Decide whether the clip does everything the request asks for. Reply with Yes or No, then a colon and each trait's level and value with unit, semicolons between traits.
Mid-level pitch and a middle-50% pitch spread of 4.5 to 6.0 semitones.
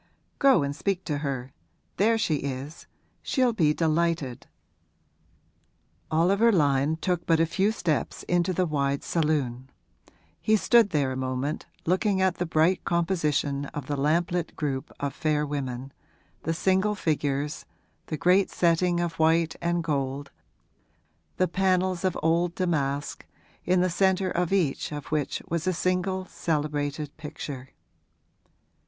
No: medium, 160 Hz; average, 4.1 semitones